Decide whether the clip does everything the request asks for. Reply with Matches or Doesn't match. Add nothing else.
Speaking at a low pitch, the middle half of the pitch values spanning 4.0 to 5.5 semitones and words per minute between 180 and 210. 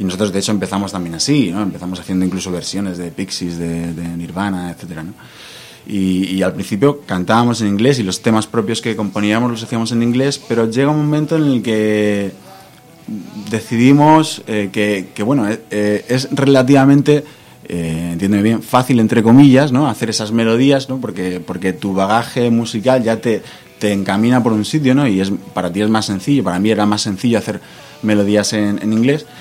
Matches